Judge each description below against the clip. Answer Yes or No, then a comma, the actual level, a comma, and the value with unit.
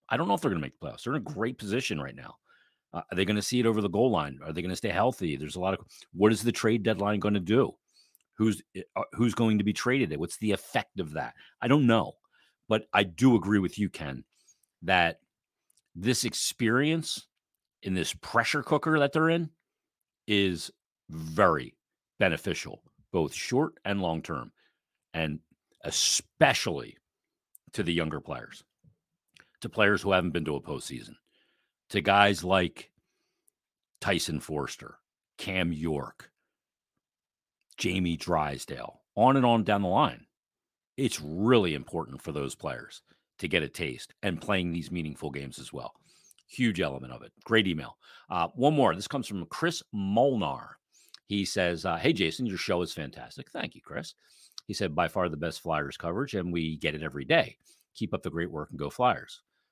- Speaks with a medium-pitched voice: No, low, 100 Hz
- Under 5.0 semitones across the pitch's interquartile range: No, average, 5.3 semitones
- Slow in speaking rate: No, average, 180 wpm